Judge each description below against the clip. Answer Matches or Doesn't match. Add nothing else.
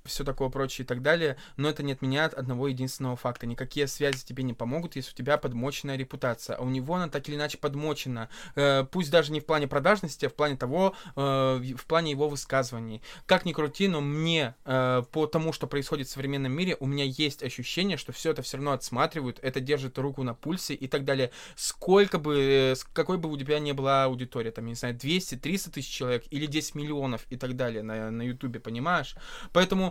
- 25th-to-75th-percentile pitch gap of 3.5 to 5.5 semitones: Doesn't match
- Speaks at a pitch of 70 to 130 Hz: Doesn't match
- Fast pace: Matches